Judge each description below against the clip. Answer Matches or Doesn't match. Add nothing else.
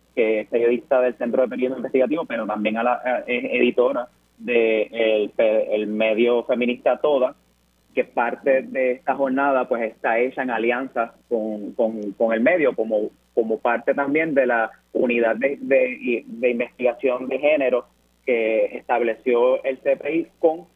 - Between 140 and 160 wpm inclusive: Matches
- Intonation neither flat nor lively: Matches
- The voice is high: Doesn't match